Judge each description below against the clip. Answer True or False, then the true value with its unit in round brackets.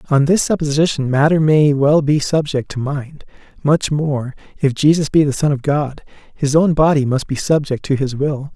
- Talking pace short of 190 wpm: False (195 wpm)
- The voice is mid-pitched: True (145 Hz)